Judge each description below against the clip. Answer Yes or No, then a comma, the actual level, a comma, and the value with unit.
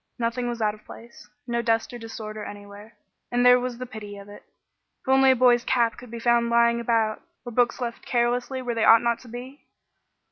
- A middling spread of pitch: No, narrow, 1.6 semitones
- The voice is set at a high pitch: Yes, high, 235 Hz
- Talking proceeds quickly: Yes, fast, 215 wpm